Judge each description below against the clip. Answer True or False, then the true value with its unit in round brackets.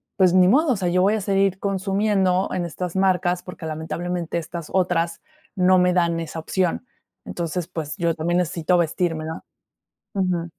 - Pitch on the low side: False (180 Hz)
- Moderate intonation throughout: False (2.0 semitones)